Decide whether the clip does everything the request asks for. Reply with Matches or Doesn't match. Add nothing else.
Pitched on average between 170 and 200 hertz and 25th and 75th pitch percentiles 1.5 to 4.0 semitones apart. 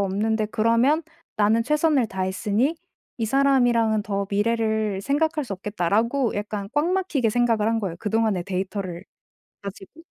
Doesn't match